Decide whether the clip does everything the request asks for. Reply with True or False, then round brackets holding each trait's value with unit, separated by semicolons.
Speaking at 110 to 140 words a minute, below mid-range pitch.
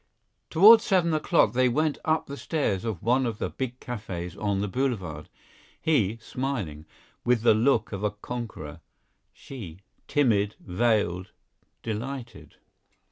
True (135 wpm; 115 Hz)